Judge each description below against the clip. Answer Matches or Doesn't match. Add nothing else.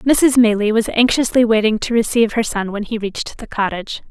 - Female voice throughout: Matches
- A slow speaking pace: Doesn't match